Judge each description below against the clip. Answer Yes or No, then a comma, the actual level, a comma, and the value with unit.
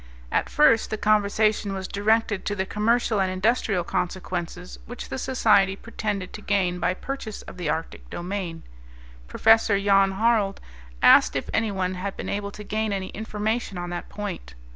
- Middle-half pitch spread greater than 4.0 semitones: No, average, 2.7 semitones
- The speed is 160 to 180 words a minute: Yes, average, 165 wpm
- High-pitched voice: Yes, high, 200 Hz